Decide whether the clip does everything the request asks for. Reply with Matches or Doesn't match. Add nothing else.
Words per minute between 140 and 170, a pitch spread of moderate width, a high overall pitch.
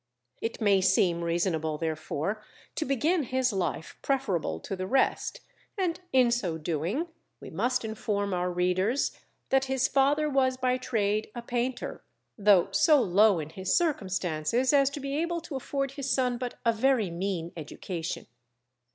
Doesn't match